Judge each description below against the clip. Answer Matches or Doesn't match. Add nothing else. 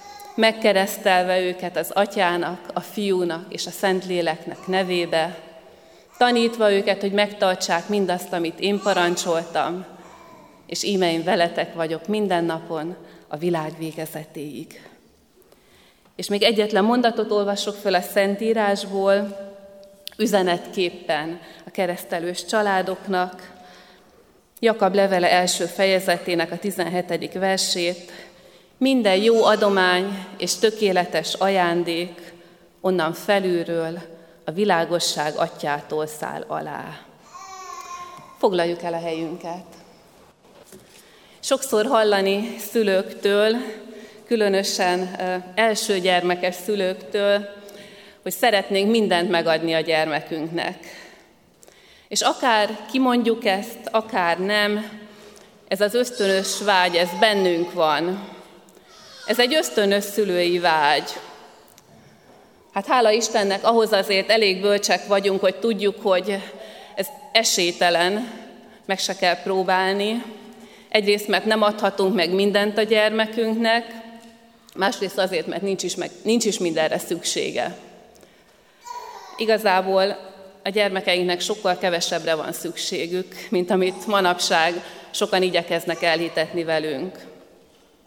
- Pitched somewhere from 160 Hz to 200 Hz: Matches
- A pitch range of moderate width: Matches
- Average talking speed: Doesn't match